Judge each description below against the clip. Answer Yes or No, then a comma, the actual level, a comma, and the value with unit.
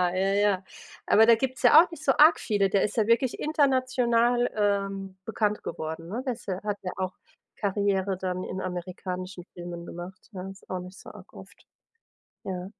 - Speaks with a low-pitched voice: No, high, 200 Hz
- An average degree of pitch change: Yes, average, 4.1 semitones